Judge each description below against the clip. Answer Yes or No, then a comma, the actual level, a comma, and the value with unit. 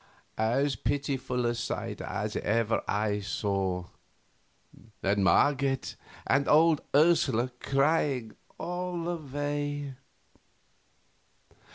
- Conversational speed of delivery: No, slow, 85 wpm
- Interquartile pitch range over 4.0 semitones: Yes, average, 4.4 semitones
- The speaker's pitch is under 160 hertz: Yes, low, 135 Hz